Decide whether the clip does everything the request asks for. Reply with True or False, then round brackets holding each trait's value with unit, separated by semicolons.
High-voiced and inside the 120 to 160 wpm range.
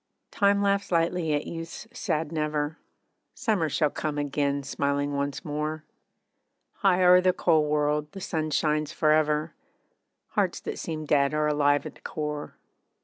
False (150 Hz; 150 wpm)